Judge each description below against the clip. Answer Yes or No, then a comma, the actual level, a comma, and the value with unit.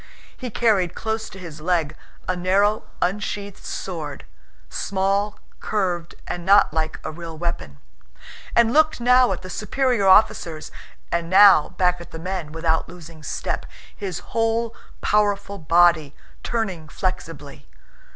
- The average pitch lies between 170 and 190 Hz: Yes, medium, 185 Hz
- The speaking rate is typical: No, slow, 130 wpm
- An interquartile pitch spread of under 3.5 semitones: No, average, 4.0 semitones